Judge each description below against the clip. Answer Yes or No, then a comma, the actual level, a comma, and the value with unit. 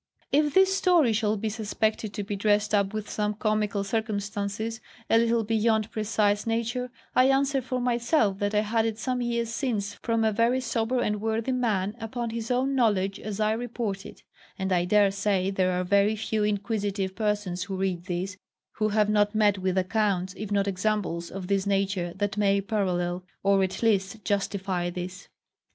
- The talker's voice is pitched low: No, high, 210 Hz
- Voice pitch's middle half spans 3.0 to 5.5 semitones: No, narrow, 2.5 semitones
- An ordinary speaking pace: Yes, average, 180 wpm